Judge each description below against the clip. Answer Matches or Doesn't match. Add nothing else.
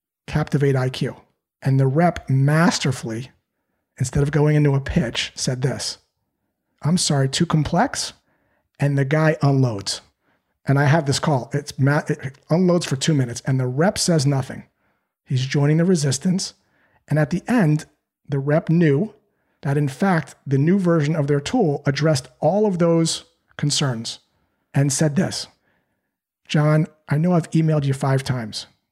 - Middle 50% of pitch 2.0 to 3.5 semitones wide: Matches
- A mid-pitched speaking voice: Matches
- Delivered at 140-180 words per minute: Matches